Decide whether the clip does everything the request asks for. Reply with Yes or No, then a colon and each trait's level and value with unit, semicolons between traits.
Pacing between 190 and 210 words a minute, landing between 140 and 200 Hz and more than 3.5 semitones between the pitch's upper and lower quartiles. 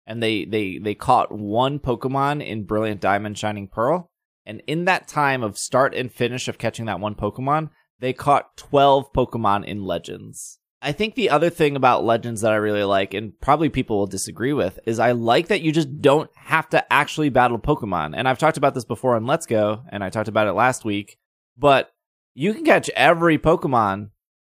No: average, 200 wpm; low, 120 Hz; wide, 5.4 semitones